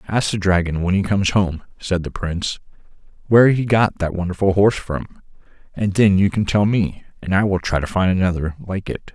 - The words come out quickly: Yes, fast, 210 wpm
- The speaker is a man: Yes, male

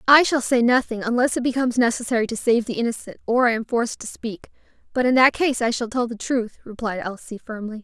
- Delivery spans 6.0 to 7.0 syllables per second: Yes, 6.1 syllables/s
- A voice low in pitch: No, high, 240 Hz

